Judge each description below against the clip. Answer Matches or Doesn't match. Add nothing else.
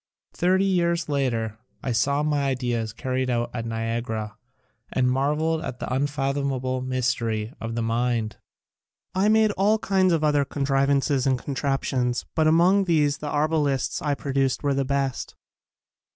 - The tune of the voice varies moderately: Matches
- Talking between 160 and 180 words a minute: Doesn't match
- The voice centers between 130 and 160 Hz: Matches